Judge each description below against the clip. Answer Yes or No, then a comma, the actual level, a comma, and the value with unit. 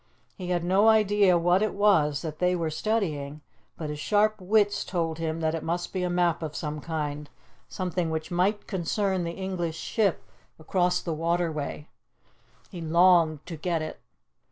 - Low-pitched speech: No, medium, 175 Hz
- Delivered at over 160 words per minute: Yes, average, 170 wpm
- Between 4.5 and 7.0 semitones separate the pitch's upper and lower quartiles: No, average, 3.0 semitones